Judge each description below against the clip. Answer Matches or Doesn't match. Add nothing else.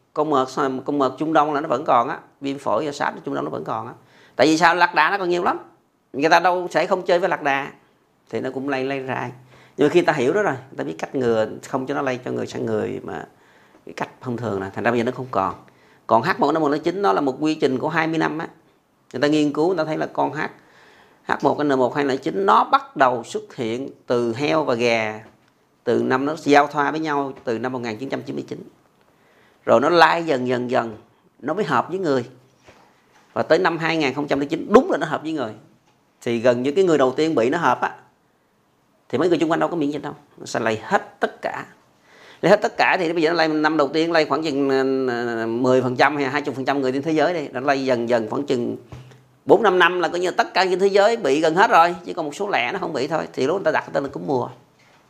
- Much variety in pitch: Doesn't match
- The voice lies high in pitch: Doesn't match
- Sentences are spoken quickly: Matches